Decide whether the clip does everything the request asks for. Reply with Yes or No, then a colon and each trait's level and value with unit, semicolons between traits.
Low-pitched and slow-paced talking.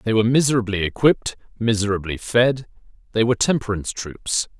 Yes: low, 110 Hz; slow, 130 wpm